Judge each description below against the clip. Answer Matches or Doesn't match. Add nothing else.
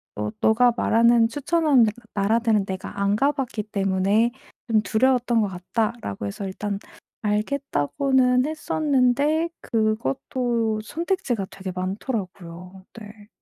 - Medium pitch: Doesn't match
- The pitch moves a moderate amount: Matches